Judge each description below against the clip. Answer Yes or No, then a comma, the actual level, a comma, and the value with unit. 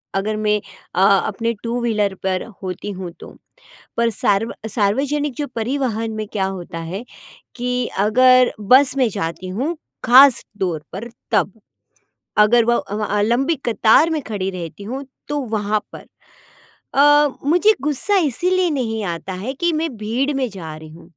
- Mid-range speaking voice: No, high, 225 Hz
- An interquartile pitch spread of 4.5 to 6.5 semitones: Yes, average, 5.2 semitones